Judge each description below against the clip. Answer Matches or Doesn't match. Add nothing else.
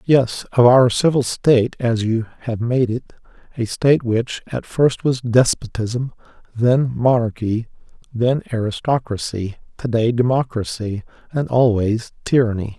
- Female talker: Doesn't match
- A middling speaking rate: Doesn't match